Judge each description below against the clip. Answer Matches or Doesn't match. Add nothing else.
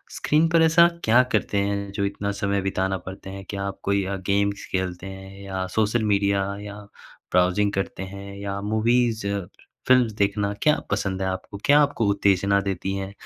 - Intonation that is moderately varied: Doesn't match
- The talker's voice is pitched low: Matches